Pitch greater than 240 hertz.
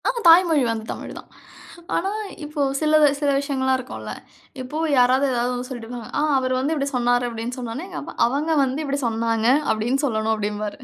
Yes: very high, 255 Hz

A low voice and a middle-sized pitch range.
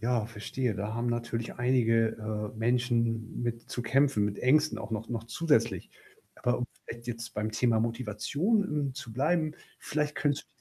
Yes: low, 120 Hz; average, 3.0 semitones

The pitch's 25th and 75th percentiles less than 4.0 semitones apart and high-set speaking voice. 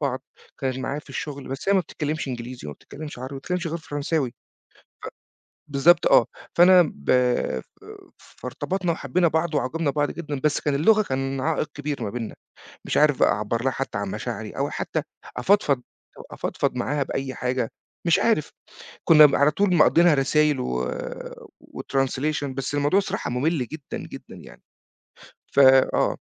No: average, 3.4 semitones; medium, 145 Hz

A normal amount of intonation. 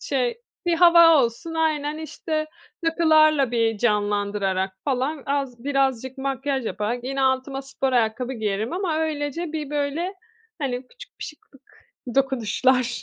Yes: average, 4.3 semitones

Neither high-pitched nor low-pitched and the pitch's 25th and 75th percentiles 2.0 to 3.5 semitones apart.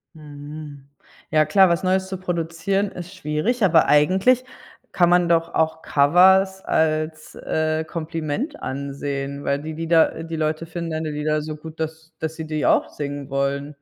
Yes: medium, 160 Hz; narrow, 2.6 semitones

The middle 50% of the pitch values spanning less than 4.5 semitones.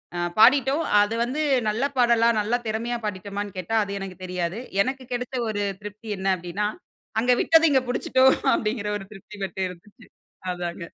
Yes: average, 4.1 semitones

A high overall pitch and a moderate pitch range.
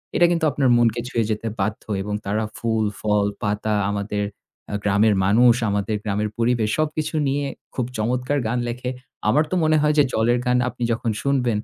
No: low, 115 Hz; average, 3.2 semitones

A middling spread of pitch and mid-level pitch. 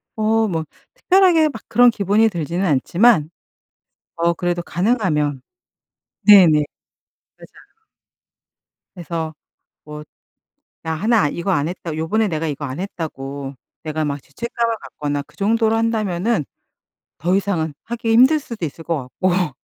No: wide, 6.2 semitones; medium, 180 Hz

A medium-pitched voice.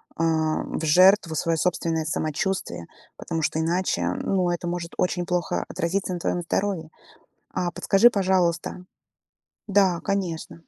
Yes: medium, 175 Hz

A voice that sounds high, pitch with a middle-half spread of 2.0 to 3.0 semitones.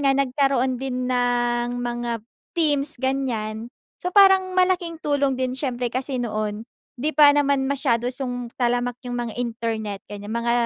Yes: very high, 250 Hz; average, 2.7 semitones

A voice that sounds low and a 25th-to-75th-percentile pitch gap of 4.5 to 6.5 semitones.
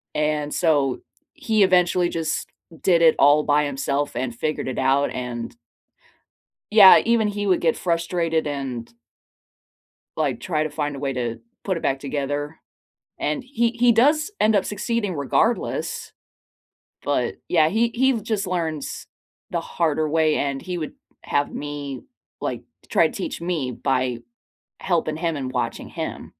No: medium, 155 Hz; average, 4.8 semitones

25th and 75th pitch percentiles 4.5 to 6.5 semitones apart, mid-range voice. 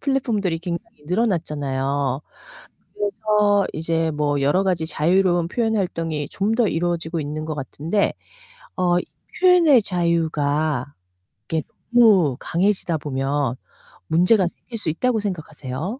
Yes: average, 5.3 semitones; medium, 170 Hz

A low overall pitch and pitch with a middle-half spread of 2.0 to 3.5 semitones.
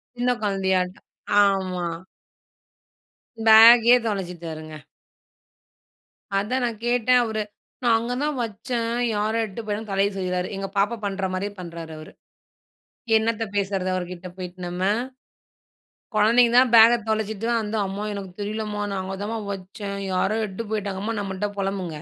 No: high, 205 Hz; average, 3.0 semitones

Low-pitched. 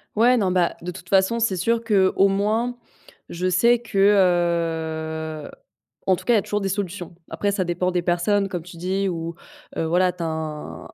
No: medium, 185 Hz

